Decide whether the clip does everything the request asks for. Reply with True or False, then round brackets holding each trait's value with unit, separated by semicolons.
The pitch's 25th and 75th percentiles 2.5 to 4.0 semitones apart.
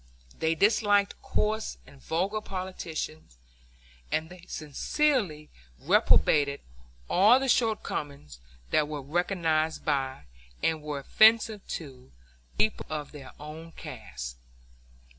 False (5.6 semitones)